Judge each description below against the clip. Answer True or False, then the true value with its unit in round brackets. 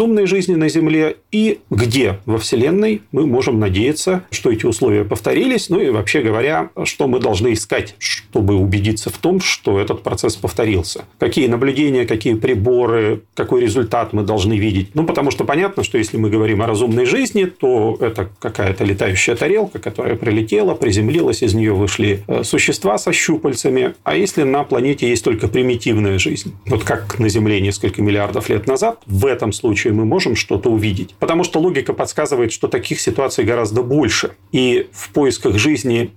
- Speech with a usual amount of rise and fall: False (6.1 semitones)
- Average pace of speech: False (170 wpm)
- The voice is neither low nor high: False (115 Hz)